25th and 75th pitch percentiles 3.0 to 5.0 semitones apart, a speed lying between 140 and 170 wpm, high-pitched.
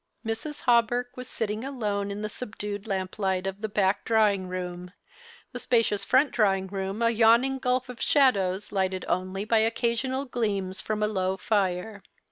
Yes: average, 3.5 semitones; average, 165 wpm; high, 210 Hz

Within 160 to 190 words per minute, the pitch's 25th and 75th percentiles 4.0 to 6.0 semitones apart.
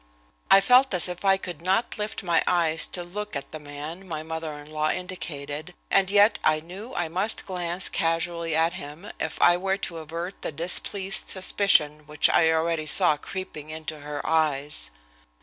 No: average, 180 wpm; average, 3.4 semitones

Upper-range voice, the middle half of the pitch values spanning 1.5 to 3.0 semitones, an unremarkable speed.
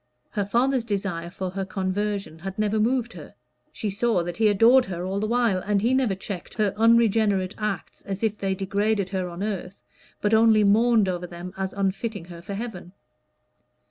Yes: high, 200 Hz; average, 2.7 semitones; average, 185 wpm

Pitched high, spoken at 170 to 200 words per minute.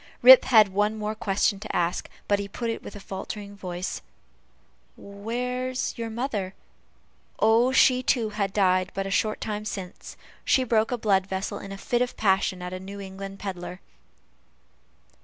Yes: high, 205 Hz; average, 175 wpm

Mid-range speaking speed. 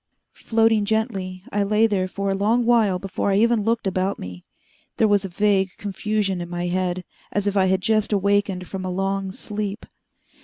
Yes: average, 190 wpm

